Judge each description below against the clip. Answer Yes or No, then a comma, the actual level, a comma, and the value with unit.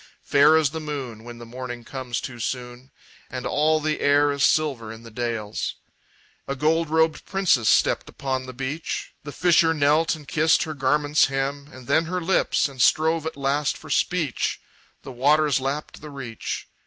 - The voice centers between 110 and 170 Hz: Yes, medium, 140 Hz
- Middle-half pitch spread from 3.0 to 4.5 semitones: Yes, average, 3.4 semitones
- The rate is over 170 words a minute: Yes, average, 180 wpm